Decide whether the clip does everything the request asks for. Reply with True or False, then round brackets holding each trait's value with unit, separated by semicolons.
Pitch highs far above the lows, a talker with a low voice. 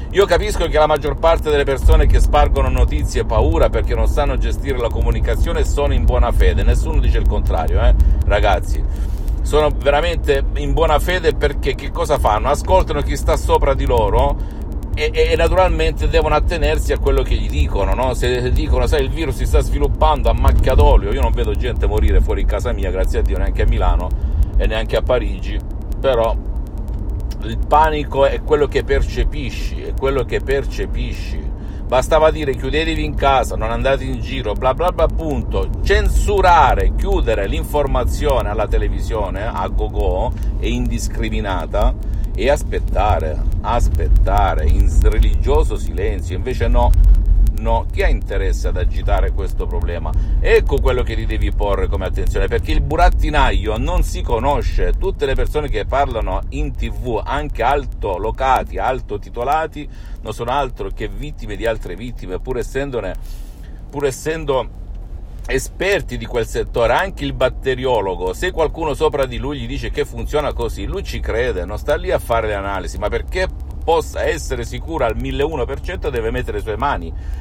True (8.9 semitones; 110 Hz)